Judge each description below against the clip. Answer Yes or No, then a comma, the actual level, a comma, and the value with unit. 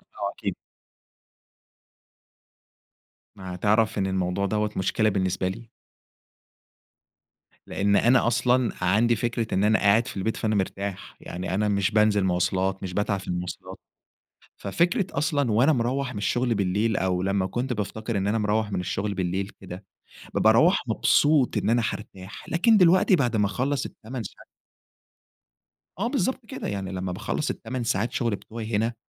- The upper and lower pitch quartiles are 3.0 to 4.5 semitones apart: Yes, average, 3.6 semitones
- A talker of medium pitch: No, low, 105 Hz